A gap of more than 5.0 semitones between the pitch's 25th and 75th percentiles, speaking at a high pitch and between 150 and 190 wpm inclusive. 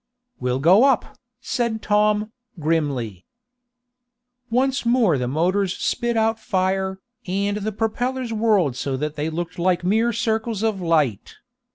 No: wide, 5.5 semitones; high, 200 Hz; slow, 135 wpm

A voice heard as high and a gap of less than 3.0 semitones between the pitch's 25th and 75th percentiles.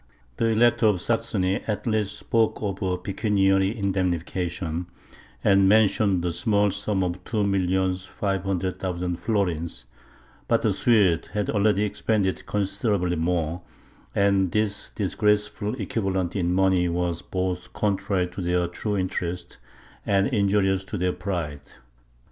No: very low, 95 Hz; narrow, 2.4 semitones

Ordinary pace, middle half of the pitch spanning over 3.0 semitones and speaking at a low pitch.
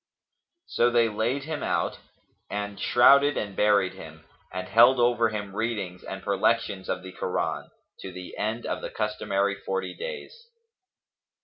Yes: average, 145 wpm; average, 3.7 semitones; low, 105 Hz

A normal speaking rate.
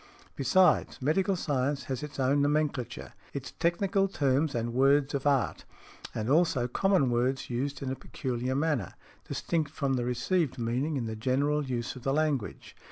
Yes: average, 165 wpm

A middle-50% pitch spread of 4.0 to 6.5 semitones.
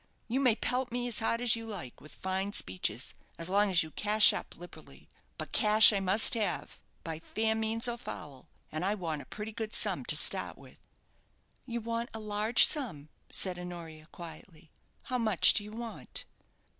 Yes: average, 4.6 semitones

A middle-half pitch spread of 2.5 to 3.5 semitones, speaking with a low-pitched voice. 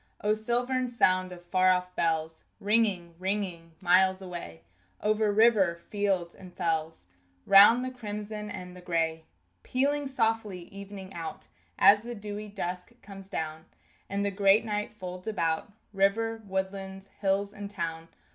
No: average, 2.9 semitones; high, 195 Hz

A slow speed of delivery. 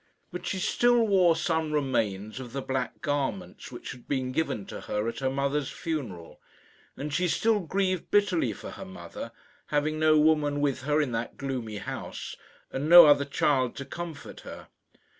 No: average, 175 wpm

